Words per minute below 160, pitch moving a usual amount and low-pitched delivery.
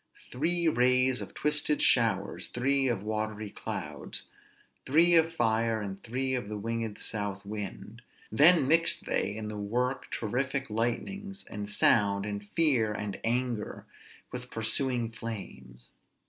Yes: slow, 135 wpm; average, 4.1 semitones; low, 115 Hz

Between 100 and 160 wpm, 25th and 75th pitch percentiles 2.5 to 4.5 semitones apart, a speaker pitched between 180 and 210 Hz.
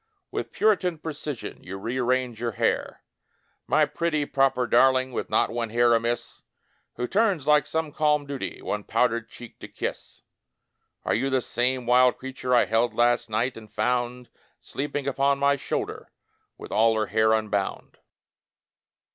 No: average, 150 wpm; average, 3.2 semitones; low, 125 Hz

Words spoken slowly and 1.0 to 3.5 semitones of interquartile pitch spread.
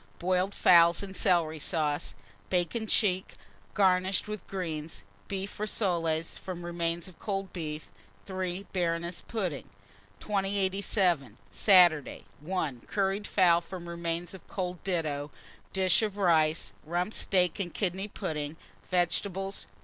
Yes: slow, 120 wpm; narrow, 2.5 semitones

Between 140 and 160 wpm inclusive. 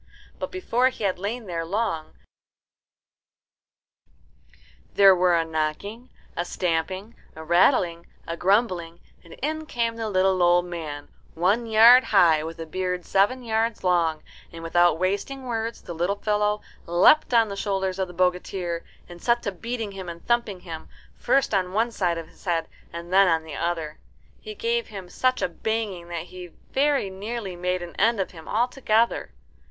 No: average, 170 wpm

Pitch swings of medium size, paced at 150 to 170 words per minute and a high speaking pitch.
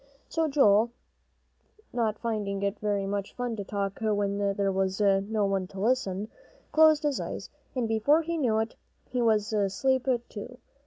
Yes: average, 3.8 semitones; average, 160 wpm; high, 215 Hz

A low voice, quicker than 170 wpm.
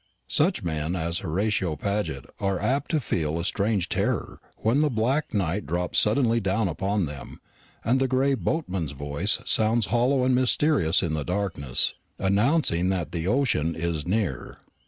No: low, 100 Hz; average, 155 wpm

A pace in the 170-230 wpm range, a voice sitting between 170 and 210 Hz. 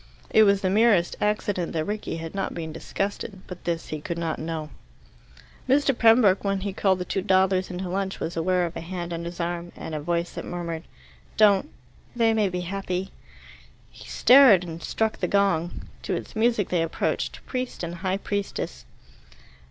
Yes: average, 185 wpm; medium, 185 Hz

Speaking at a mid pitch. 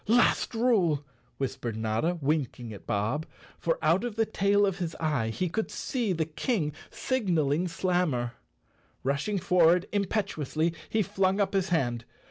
Yes: medium, 170 Hz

